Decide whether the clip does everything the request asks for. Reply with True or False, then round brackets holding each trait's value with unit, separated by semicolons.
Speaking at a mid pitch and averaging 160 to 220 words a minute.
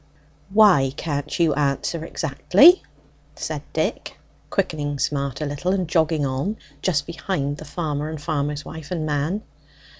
False (155 Hz; 140 wpm)